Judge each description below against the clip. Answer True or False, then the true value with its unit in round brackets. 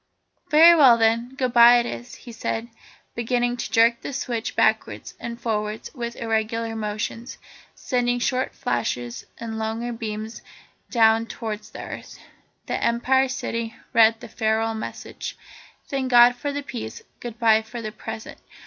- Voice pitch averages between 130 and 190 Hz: False (230 Hz)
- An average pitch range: False (1.6 semitones)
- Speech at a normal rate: True (145 wpm)